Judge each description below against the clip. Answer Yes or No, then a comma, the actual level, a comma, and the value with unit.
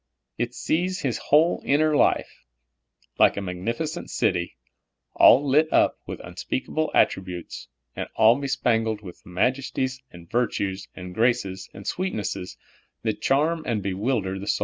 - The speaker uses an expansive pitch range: Yes, wide, 6.7 semitones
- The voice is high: No, low, 115 Hz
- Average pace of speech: No, slow, 130 wpm